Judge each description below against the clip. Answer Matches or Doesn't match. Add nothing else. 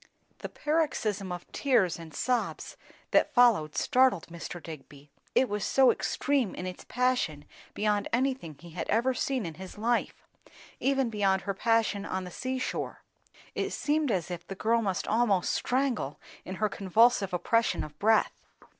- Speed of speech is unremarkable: Matches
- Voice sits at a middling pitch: Doesn't match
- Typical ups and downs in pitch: Doesn't match